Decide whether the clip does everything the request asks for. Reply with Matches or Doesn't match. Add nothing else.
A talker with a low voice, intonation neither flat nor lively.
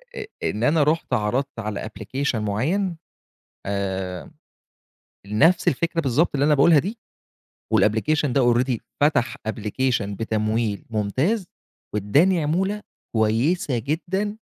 Doesn't match